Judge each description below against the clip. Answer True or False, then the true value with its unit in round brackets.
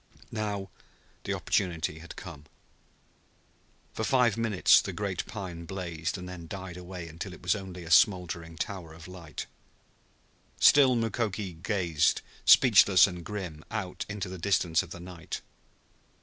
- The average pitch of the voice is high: False (90 Hz)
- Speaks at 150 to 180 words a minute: False (140 wpm)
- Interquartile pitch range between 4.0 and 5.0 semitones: False (3.2 semitones)